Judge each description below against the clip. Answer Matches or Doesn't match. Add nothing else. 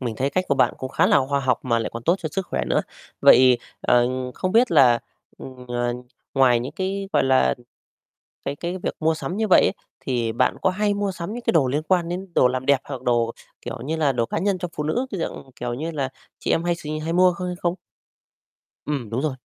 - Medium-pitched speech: Matches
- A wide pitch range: Matches